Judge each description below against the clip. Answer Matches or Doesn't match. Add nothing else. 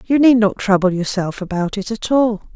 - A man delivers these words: Doesn't match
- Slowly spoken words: Doesn't match